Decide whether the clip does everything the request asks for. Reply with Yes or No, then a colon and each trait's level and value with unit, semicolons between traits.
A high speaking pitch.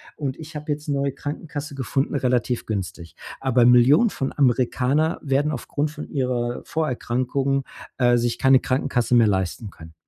No: low, 130 Hz